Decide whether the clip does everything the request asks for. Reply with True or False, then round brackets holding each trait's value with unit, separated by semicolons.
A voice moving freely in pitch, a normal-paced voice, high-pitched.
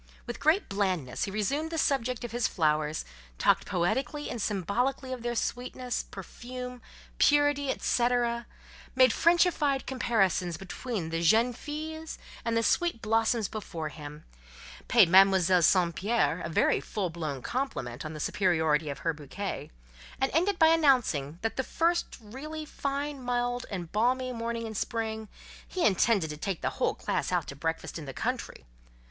True (6.7 semitones; 155 wpm; 230 Hz)